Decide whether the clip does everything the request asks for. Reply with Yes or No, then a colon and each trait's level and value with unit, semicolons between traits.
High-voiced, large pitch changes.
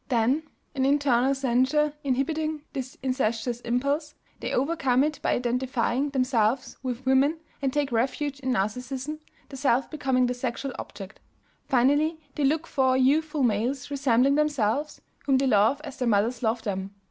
No: very high, 265 Hz; average, 2.7 semitones